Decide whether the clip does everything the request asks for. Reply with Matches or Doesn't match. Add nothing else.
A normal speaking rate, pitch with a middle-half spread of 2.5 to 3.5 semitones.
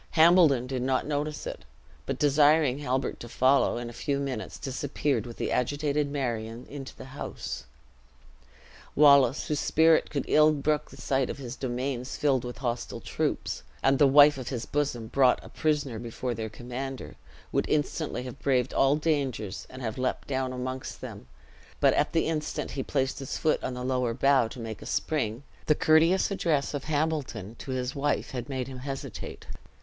Matches